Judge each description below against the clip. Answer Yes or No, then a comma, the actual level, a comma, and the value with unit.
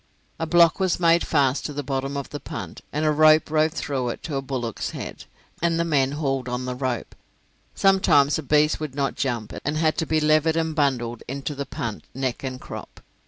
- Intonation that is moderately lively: Yes, average, 3.0 semitones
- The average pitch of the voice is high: No, medium, 145 Hz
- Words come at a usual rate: No, fast, 210 wpm